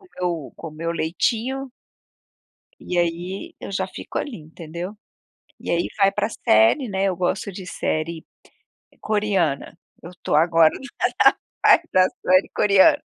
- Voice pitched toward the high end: No, medium, 180 Hz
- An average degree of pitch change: Yes, average, 3.2 semitones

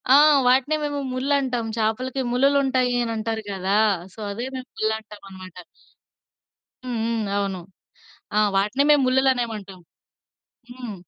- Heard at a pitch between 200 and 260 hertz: Yes, high, 240 Hz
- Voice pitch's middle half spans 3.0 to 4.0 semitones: Yes, average, 3.7 semitones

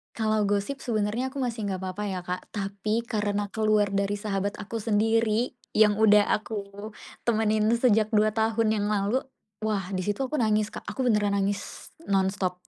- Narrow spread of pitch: Yes, narrow, 1.6 semitones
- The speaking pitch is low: No, high, 210 Hz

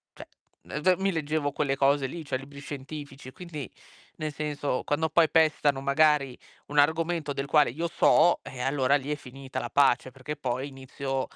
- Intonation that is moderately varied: No, narrow, 2.2 semitones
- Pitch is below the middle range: No, medium, 145 Hz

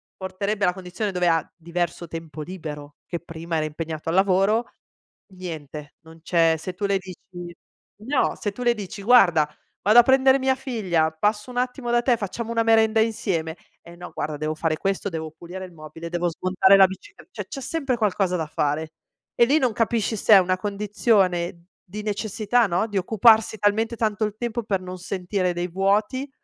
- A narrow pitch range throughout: No, average, 4.5 semitones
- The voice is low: No, high, 190 Hz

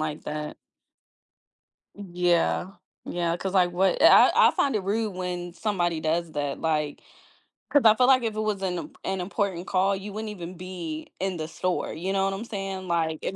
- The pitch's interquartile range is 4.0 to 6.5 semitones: No, average, 2.8 semitones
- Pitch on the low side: No, medium, 185 Hz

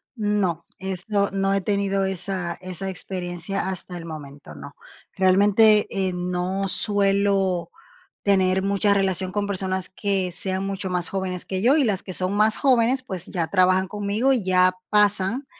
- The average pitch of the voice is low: No, high, 190 Hz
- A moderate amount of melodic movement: No, narrow, 1.8 semitones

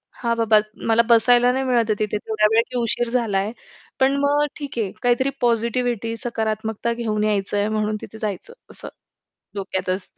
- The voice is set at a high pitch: Yes, high, 230 Hz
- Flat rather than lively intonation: Yes, narrow, 2.3 semitones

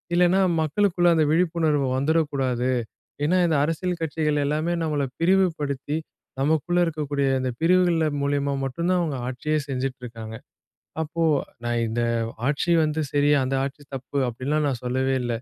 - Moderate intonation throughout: Yes, average, 3.6 semitones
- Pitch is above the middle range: No, medium, 150 Hz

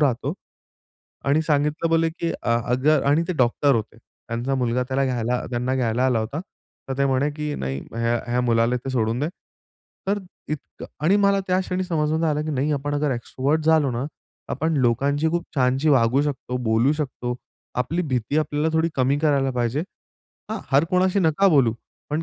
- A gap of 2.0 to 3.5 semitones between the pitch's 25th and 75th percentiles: No, average, 4.0 semitones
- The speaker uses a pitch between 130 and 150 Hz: Yes, medium, 140 Hz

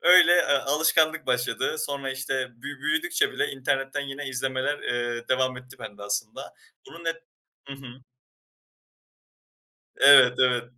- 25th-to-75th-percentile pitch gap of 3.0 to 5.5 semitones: No, narrow, 2.4 semitones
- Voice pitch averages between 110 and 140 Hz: Yes, low, 135 Hz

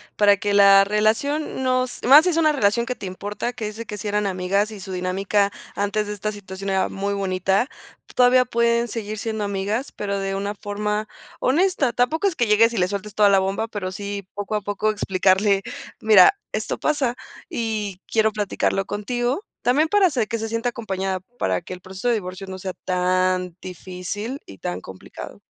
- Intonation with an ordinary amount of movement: Yes, average, 3.2 semitones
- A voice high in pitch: Yes, high, 205 Hz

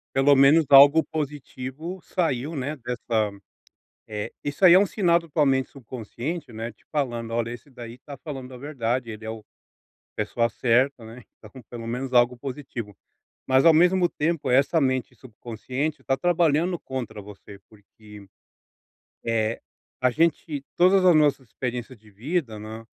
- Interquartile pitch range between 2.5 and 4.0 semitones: No, average, 4.7 semitones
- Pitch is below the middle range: Yes, low, 130 Hz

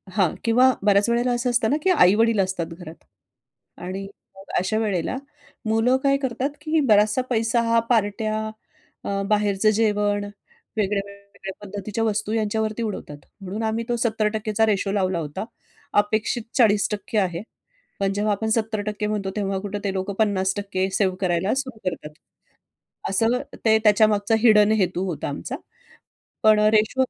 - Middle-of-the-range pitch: No, high, 210 Hz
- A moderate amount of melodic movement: No, narrow, 2.2 semitones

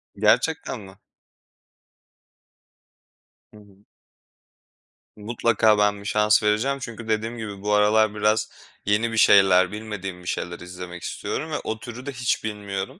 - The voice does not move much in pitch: Yes, narrow, 1.9 semitones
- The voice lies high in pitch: No, low, 105 Hz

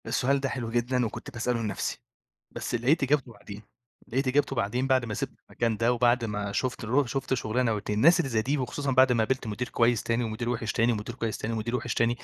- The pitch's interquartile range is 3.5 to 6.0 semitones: No, narrow, 2.5 semitones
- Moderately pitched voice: No, low, 120 Hz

